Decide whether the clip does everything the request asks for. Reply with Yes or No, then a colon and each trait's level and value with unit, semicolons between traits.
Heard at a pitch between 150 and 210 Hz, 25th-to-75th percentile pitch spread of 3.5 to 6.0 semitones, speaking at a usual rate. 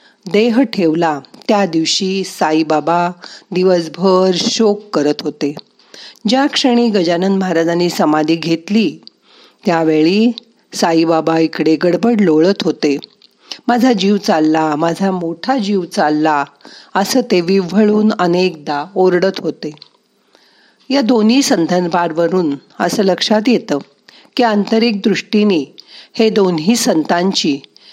Yes: medium, 185 Hz; average, 4.9 semitones; average, 100 wpm